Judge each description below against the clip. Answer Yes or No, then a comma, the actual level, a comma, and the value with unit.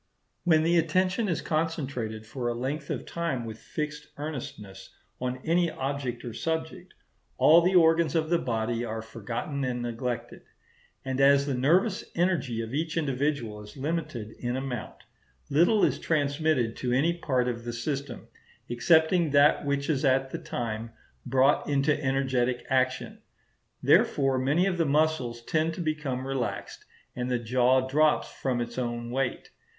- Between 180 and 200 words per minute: No, average, 155 wpm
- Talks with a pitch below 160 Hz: Yes, low, 135 Hz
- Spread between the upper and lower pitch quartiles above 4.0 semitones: Yes, average, 4.4 semitones